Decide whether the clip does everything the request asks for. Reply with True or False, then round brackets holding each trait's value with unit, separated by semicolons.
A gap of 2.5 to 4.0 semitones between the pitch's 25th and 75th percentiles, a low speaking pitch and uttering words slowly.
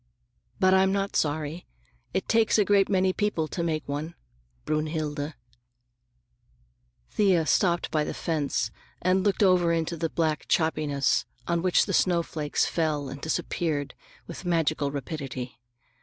False (3.7 semitones; 160 Hz; 130 wpm)